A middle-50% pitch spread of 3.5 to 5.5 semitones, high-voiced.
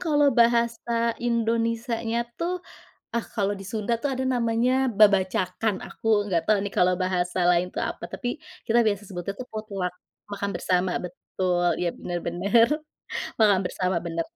Yes: average, 4.2 semitones; high, 210 Hz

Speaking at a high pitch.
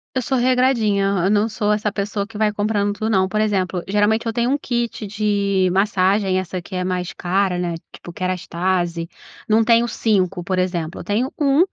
Yes: high, 205 Hz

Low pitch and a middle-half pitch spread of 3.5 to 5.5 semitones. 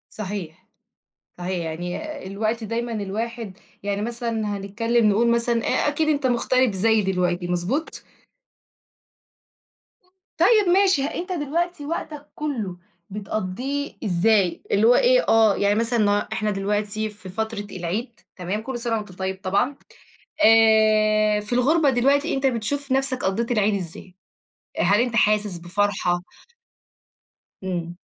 No: high, 220 Hz; average, 4.2 semitones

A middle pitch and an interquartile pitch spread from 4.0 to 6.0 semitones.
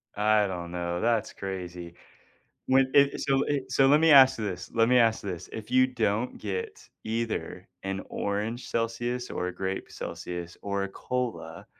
No: low, 110 Hz; average, 4.7 semitones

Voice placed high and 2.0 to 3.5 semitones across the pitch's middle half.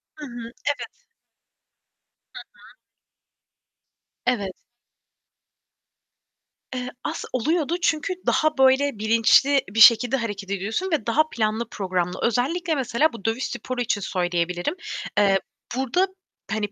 No: high, 240 Hz; wide, 5.6 semitones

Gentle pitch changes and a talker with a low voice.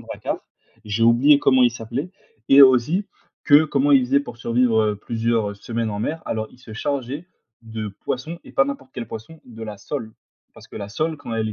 No: average, 4.0 semitones; low, 120 Hz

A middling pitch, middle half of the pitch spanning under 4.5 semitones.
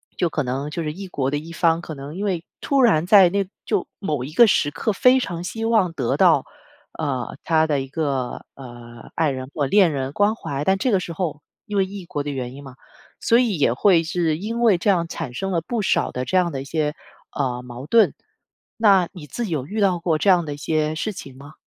No: medium, 165 Hz; wide, 5.5 semitones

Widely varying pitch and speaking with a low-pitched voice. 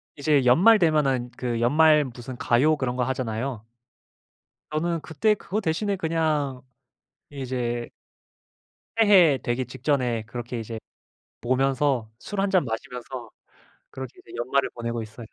No: average, 4.4 semitones; low, 130 Hz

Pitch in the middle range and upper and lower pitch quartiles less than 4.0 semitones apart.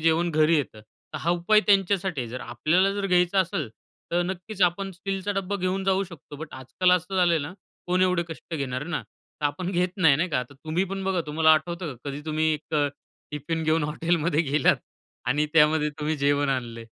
Yes: medium, 165 Hz; average, 3.6 semitones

